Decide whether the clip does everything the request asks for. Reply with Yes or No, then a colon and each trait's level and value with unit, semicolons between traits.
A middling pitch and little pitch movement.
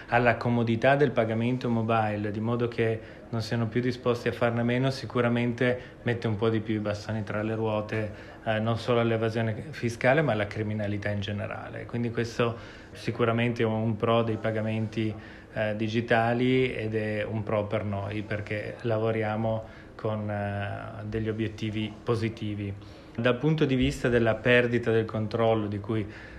No: low, 110 Hz; narrow, 1.8 semitones